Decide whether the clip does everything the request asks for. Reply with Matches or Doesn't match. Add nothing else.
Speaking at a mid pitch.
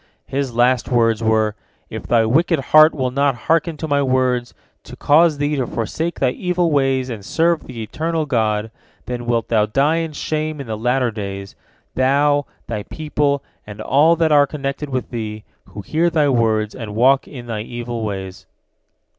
Doesn't match